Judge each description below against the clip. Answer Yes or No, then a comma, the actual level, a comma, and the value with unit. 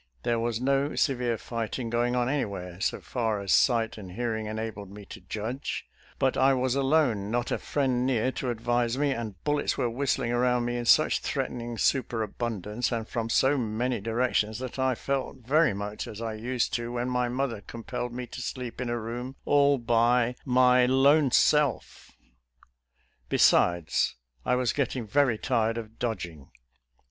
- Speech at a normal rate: Yes, average, 175 wpm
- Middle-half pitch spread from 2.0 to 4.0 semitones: Yes, narrow, 2.4 semitones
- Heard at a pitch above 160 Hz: No, low, 120 Hz